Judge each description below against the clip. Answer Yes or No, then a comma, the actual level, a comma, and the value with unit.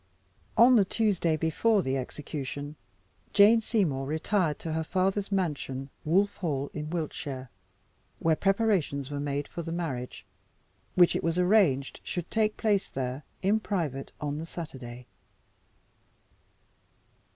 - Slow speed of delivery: Yes, slow, 130 wpm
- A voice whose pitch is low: No, medium, 160 Hz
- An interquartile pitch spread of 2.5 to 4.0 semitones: No, wide, 5.6 semitones